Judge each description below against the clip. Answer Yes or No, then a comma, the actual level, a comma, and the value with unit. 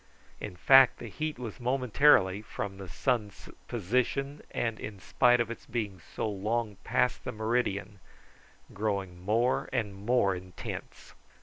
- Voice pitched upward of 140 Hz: No, low, 110 Hz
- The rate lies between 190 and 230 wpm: No, slow, 135 wpm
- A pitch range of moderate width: Yes, average, 3.9 semitones